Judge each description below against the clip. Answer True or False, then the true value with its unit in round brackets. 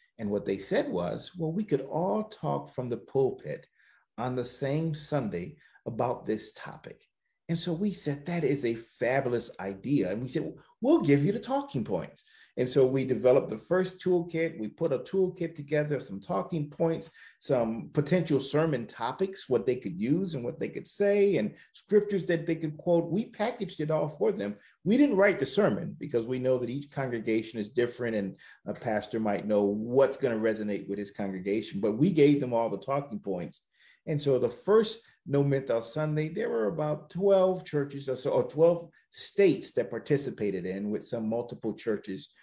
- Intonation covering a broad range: True (7.3 semitones)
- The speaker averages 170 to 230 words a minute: True (190 wpm)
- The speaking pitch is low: False (150 Hz)